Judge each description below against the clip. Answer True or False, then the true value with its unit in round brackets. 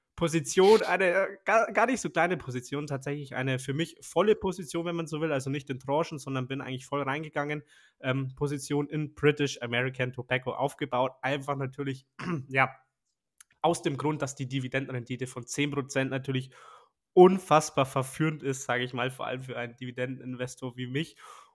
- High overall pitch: False (135 Hz)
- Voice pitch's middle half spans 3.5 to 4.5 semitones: False (2.8 semitones)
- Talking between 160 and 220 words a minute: True (165 wpm)